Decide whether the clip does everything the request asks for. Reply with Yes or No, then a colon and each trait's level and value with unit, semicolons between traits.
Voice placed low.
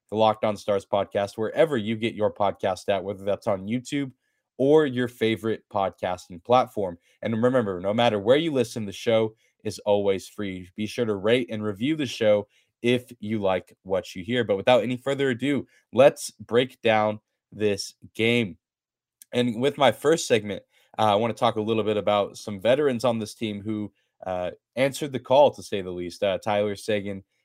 Yes: low, 110 Hz